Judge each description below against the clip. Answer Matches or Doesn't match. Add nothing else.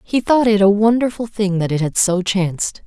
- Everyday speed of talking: Doesn't match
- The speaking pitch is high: Matches